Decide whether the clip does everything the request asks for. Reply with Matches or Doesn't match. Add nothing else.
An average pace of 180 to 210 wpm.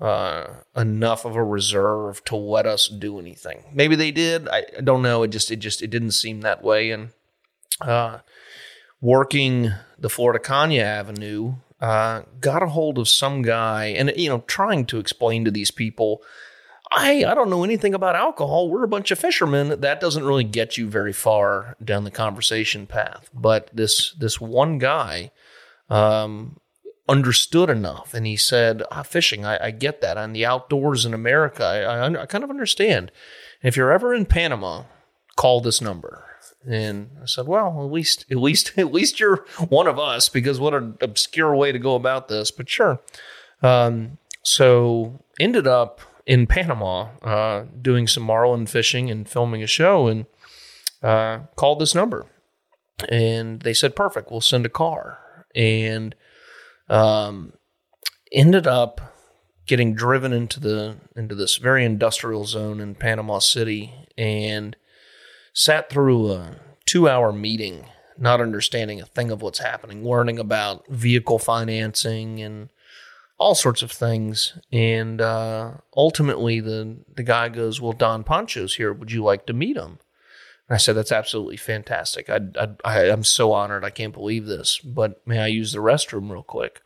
Doesn't match